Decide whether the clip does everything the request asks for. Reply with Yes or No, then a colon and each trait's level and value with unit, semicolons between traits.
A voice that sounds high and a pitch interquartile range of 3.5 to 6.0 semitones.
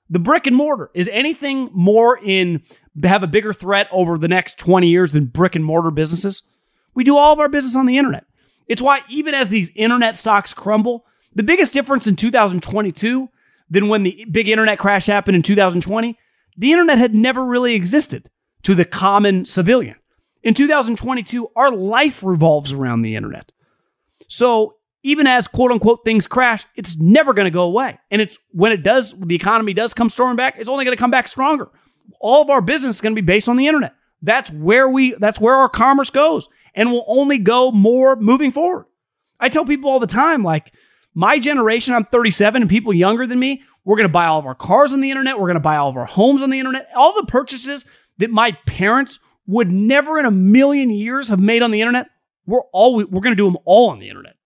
Yes: high, 230 Hz; average, 5.0 semitones